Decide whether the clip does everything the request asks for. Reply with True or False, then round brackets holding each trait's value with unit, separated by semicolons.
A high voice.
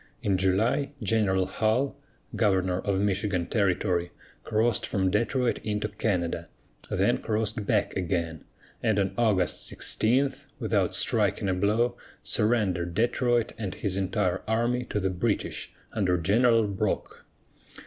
False (105 Hz)